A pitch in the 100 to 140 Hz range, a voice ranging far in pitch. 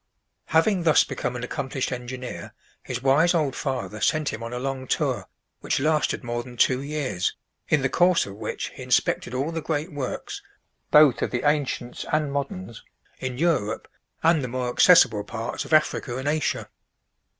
No: low, 135 Hz; average, 3.9 semitones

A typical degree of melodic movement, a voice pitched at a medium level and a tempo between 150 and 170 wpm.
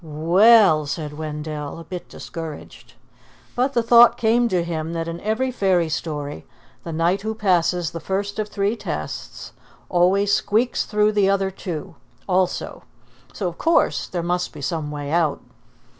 Yes: average, 4.6 semitones; medium, 180 Hz; average, 160 wpm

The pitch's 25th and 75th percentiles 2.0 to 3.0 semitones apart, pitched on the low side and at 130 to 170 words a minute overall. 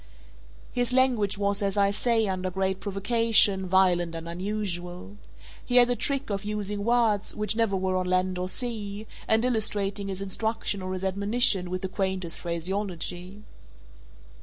No: average, 2.7 semitones; high, 200 Hz; average, 155 wpm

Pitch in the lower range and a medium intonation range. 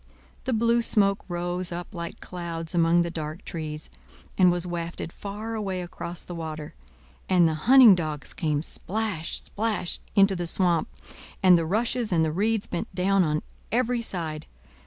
No: medium, 175 Hz; average, 3.6 semitones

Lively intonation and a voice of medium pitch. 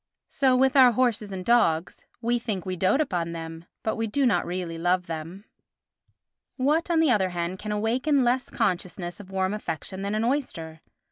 No: wide, 5.8 semitones; high, 205 Hz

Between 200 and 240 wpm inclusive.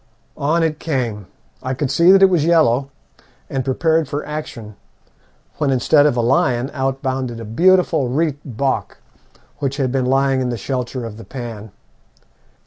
No: average, 165 wpm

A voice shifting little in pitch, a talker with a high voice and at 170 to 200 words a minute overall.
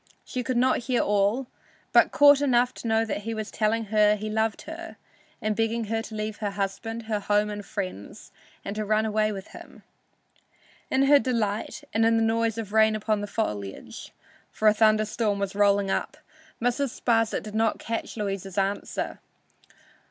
Yes: narrow, 1.7 semitones; high, 215 Hz; average, 180 wpm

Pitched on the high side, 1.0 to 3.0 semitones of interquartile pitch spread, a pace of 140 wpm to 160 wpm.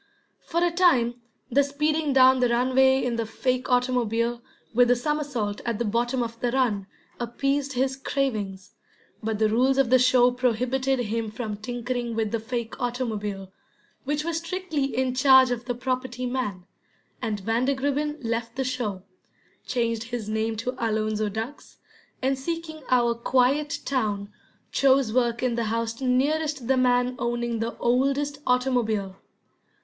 Yes: high, 245 Hz; narrow, 2.6 semitones; average, 150 wpm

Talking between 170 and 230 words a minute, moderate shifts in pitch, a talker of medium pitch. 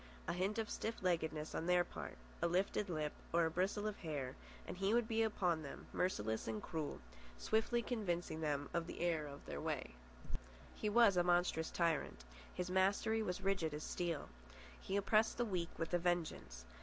Yes: average, 185 wpm; average, 4.1 semitones; medium, 175 Hz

